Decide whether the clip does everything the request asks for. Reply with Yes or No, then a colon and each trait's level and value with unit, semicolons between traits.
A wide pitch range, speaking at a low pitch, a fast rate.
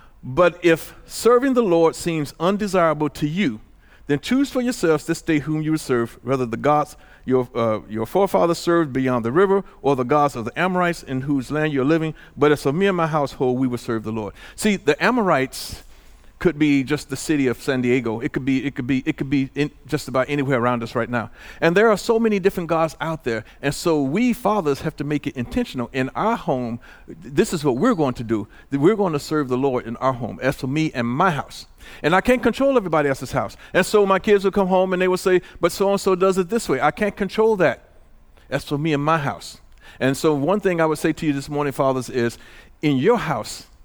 No: wide, 5.7 semitones; medium, 150 Hz; fast, 240 wpm